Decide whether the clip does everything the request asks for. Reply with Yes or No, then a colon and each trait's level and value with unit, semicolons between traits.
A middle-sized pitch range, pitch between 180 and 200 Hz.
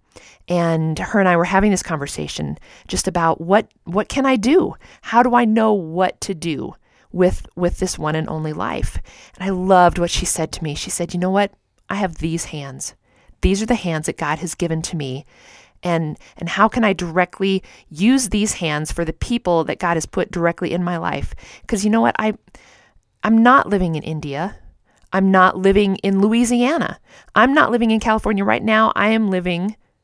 Yes: average, 4.2 semitones; medium, 185 Hz